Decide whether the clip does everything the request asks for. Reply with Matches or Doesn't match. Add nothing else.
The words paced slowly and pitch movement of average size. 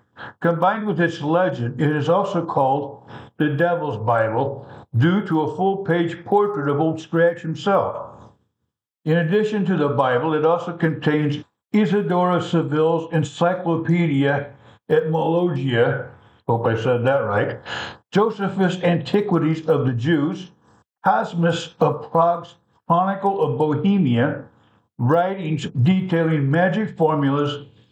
Matches